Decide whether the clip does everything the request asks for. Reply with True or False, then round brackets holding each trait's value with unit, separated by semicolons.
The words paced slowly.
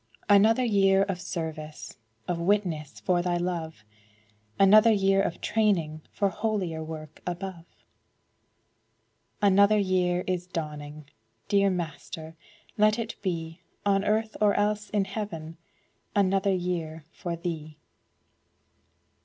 True (110 wpm)